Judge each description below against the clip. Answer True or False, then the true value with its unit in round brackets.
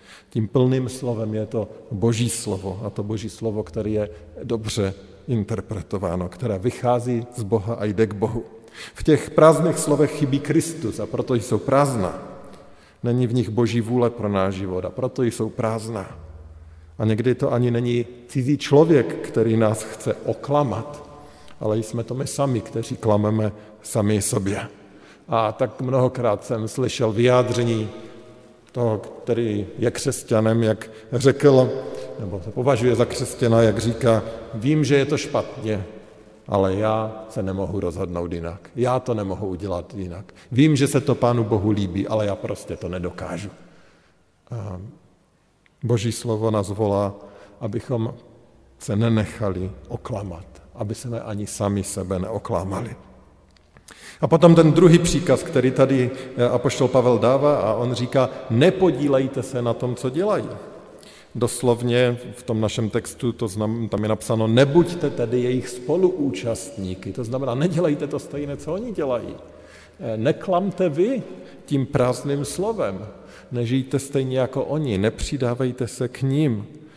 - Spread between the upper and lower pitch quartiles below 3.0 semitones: False (3.3 semitones)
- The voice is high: False (115 Hz)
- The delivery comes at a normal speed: True (140 wpm)